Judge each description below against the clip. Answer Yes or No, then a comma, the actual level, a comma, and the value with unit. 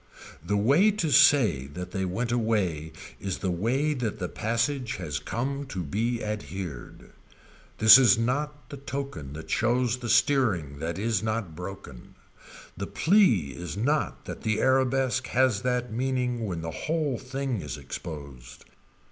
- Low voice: Yes, low, 115 Hz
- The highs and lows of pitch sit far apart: Yes, wide, 6.7 semitones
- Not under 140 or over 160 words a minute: Yes, average, 150 wpm